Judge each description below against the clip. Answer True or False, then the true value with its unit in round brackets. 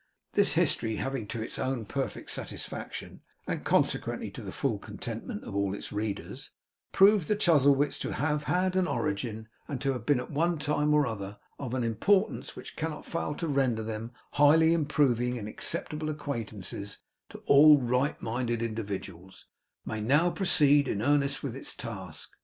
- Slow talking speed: False (165 wpm)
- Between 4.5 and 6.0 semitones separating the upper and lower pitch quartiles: True (5.1 semitones)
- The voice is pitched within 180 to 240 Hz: False (135 Hz)